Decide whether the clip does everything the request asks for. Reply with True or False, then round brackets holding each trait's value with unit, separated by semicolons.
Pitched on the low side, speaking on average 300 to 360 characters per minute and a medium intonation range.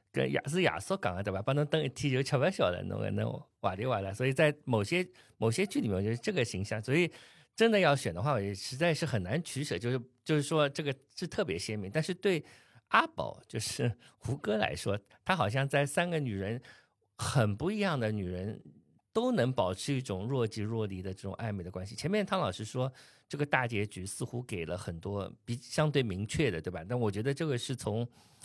False (125 Hz; 315 characters per minute; 6.0 semitones)